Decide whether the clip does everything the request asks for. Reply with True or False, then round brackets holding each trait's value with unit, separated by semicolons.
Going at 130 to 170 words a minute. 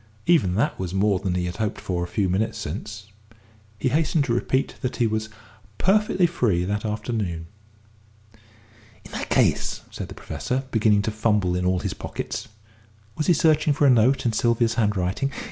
False (180 wpm)